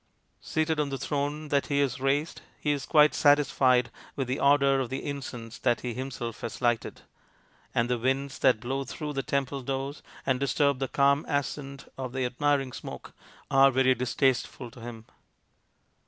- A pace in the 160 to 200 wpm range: Yes, average, 170 wpm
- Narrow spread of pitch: Yes, narrow, 2.0 semitones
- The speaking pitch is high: No, low, 135 Hz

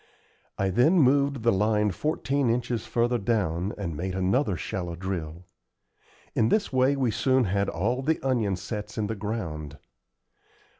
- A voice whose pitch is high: No, low, 110 Hz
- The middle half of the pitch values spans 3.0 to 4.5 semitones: No, wide, 5.4 semitones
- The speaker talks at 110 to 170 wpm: Yes, average, 150 wpm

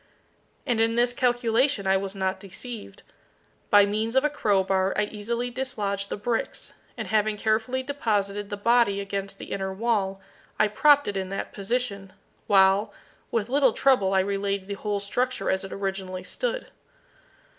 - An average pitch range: Yes, average, 3.5 semitones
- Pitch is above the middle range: Yes, high, 205 Hz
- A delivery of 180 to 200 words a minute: No, average, 160 wpm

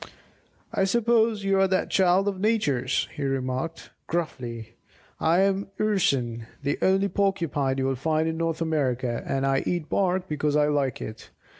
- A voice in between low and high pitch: Yes, medium, 160 Hz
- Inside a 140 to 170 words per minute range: Yes, average, 160 wpm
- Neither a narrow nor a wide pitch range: No, wide, 6.1 semitones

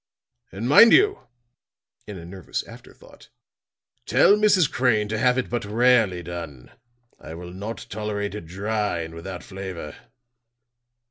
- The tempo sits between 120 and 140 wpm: Yes, slow, 135 wpm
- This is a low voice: Yes, low, 105 Hz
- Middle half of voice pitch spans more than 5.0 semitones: Yes, wide, 5.5 semitones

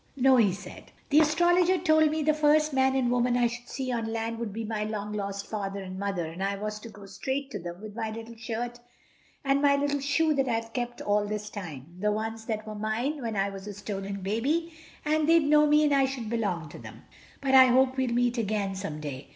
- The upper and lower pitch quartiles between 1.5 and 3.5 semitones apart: No, average, 5.0 semitones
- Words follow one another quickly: Yes, fast, 235 wpm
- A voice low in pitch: No, high, 230 Hz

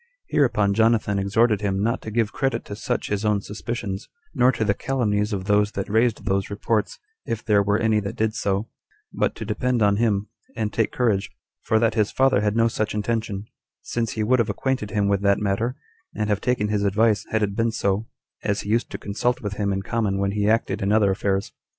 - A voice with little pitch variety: Yes, narrow, 2.1 semitones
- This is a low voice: Yes, low, 105 Hz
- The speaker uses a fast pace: Yes, fast, 220 wpm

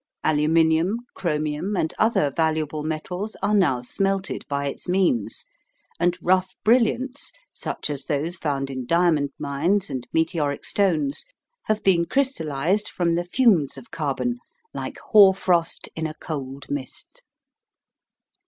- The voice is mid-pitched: Yes, medium, 165 Hz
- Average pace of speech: No, slow, 130 wpm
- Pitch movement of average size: Yes, average, 4.8 semitones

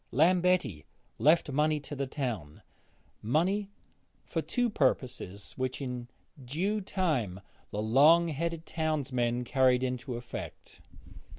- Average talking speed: No, slow, 110 wpm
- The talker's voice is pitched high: No, medium, 140 Hz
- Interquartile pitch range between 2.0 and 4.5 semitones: No, average, 5.2 semitones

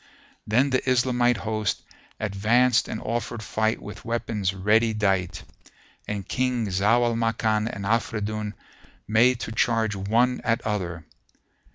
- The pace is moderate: No, slow, 130 wpm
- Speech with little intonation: Yes, narrow, 2.2 semitones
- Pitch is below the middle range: Yes, low, 110 Hz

